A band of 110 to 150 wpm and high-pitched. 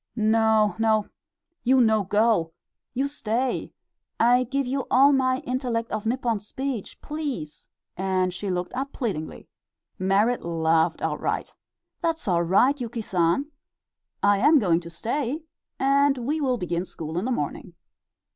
Yes: average, 140 wpm; high, 225 Hz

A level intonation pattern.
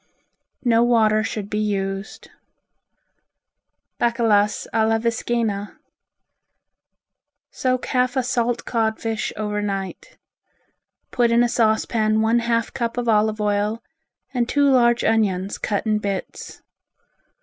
Yes: narrow, 2.1 semitones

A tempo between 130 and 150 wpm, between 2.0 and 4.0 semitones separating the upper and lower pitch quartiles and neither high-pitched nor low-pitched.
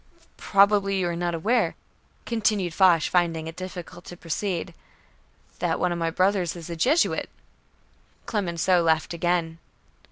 Yes: slow, 135 wpm; average, 2.7 semitones; medium, 175 Hz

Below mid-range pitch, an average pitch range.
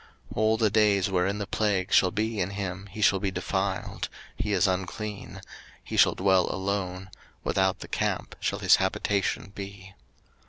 No: low, 100 Hz; narrow, 1.5 semitones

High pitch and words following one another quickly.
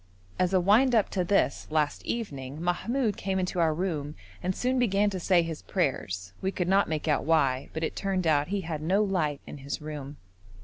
No: medium, 175 Hz; fast, 210 wpm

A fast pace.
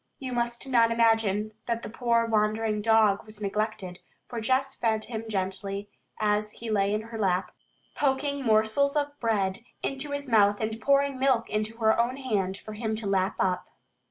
No: average, 175 wpm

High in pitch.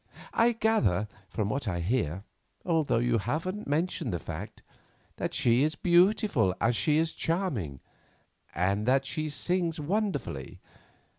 No: medium, 140 Hz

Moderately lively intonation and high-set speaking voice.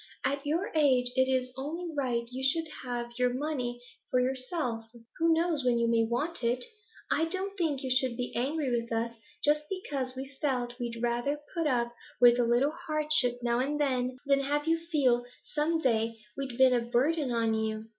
Yes: average, 3.7 semitones; very high, 260 Hz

